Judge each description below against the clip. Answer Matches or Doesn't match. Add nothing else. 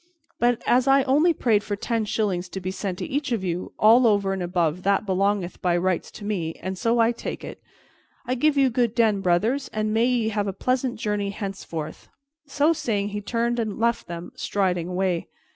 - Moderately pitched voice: Doesn't match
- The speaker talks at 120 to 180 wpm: Doesn't match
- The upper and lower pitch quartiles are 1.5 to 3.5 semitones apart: Doesn't match